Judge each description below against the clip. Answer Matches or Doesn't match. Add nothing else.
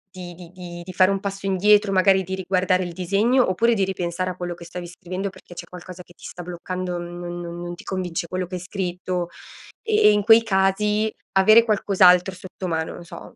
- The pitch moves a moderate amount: Doesn't match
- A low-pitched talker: Doesn't match